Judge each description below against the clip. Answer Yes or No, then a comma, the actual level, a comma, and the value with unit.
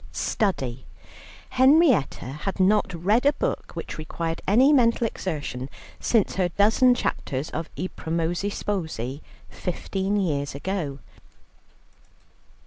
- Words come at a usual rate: No, slow, 110 wpm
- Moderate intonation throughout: No, wide, 5.8 semitones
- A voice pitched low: No, medium, 185 Hz